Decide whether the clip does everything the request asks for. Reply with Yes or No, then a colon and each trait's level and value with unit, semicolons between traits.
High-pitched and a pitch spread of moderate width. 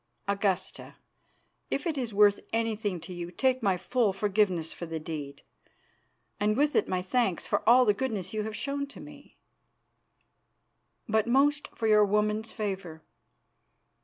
Yes: high, 210 Hz; average, 4.4 semitones